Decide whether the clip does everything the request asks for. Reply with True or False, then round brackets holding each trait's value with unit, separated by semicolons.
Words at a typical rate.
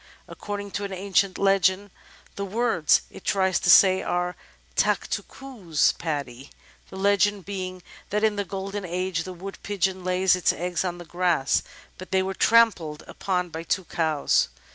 True (165 wpm)